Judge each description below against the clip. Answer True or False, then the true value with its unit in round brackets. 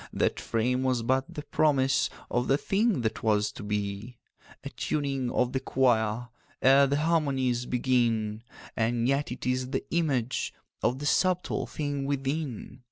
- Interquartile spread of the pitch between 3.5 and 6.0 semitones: False (3.0 semitones)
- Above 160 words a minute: False (155 wpm)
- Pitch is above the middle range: False (130 Hz)